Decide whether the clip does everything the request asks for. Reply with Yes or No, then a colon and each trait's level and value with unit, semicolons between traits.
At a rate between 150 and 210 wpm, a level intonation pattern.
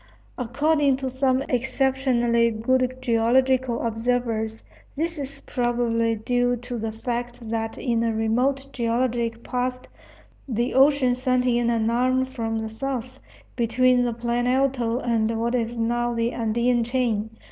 No: slow, 135 wpm; narrow, 2.0 semitones